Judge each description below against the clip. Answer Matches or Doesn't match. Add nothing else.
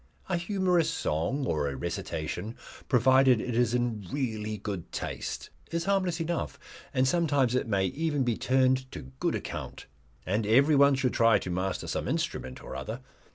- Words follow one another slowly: Doesn't match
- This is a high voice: Doesn't match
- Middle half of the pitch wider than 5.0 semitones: Matches